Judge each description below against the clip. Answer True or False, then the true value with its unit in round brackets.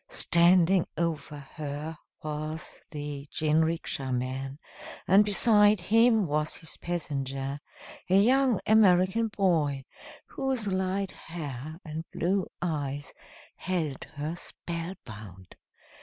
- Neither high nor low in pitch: True (165 Hz)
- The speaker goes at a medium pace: False (100 wpm)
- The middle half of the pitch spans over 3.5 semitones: True (4.8 semitones)